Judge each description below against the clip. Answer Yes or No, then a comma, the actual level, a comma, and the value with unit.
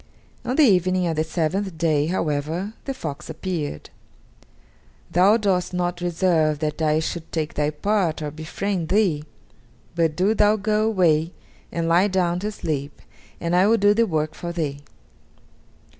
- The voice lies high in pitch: No, medium, 175 Hz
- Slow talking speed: No, average, 160 wpm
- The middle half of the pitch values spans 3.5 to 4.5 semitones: Yes, average, 3.9 semitones